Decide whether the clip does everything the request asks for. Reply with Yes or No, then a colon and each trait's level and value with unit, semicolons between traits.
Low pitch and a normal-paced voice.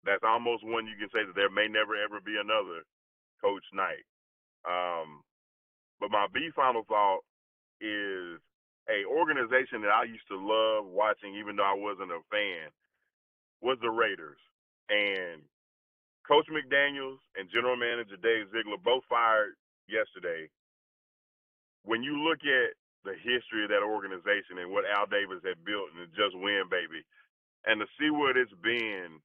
Yes: low, 120 Hz; average, 155 wpm